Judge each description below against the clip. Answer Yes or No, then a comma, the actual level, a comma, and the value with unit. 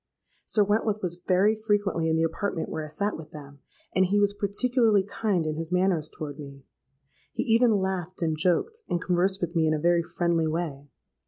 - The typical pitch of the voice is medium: Yes, medium, 180 Hz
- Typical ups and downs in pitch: Yes, average, 4.1 semitones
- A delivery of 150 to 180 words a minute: No, average, 195 wpm